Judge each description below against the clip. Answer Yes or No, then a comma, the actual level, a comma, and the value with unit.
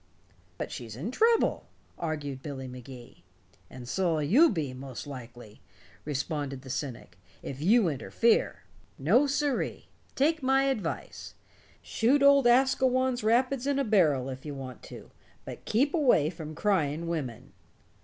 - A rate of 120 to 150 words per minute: Yes, slow, 135 wpm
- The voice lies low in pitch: No, medium, 165 Hz